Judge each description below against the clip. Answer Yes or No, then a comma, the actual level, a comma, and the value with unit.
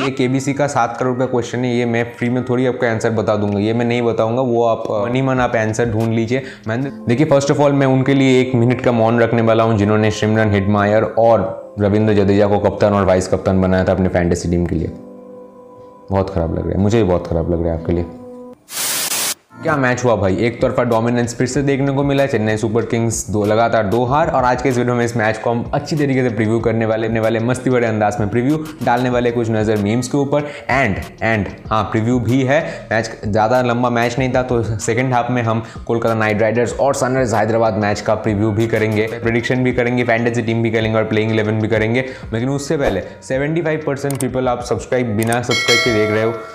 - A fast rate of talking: Yes, fast, 225 wpm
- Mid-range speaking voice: No, low, 115 Hz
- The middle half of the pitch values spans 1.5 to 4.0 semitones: Yes, average, 2.7 semitones